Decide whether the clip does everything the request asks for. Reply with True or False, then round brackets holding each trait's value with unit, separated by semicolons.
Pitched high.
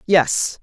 False (170 Hz)